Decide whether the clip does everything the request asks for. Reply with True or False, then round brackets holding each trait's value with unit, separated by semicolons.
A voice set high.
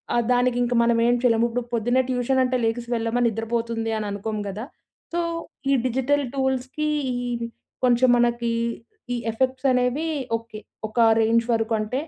True (240 Hz)